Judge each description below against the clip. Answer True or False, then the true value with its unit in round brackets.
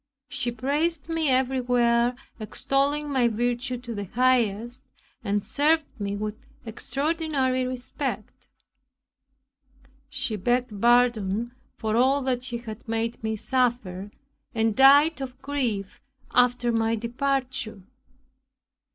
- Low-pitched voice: False (245 Hz)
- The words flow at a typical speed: False (110 wpm)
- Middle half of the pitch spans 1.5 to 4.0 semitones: True (3.0 semitones)